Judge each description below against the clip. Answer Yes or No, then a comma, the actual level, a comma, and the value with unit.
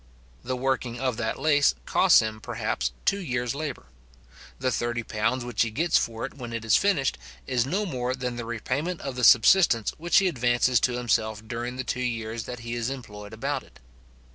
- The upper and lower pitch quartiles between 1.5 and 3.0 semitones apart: Yes, average, 2.7 semitones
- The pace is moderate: Yes, average, 190 wpm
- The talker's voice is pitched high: No, low, 125 Hz